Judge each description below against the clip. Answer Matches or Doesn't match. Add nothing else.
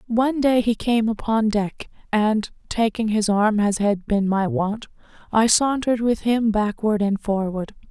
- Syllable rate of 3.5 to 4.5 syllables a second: Matches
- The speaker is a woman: Matches